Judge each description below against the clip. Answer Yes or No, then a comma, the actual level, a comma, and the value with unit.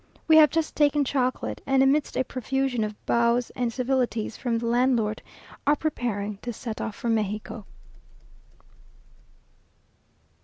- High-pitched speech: Yes, high, 245 Hz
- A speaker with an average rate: No, slow, 130 wpm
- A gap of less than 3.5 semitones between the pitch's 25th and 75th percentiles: Yes, average, 3.1 semitones